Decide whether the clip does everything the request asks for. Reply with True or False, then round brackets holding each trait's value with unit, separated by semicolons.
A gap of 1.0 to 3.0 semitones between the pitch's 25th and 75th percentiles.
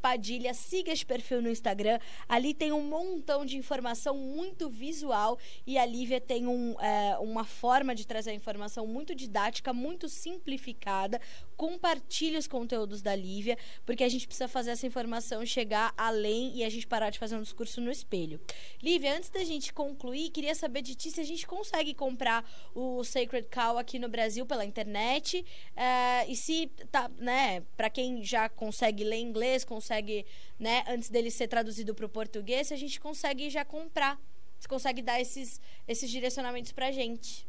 False (3.7 semitones)